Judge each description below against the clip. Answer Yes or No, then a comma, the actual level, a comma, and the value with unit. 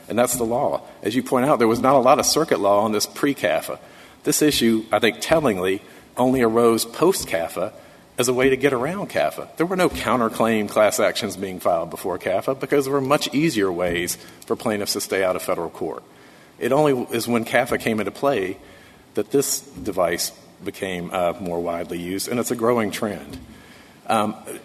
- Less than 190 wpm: No, average, 200 wpm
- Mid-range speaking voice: No, low, 115 Hz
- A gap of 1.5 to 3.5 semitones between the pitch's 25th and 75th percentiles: No, average, 4.9 semitones